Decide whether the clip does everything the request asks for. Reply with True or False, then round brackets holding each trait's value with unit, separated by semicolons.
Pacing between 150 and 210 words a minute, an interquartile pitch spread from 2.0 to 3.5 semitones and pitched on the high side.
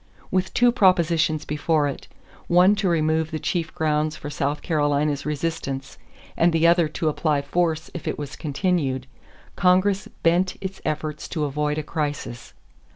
False (155 wpm; 2.8 semitones; 155 Hz)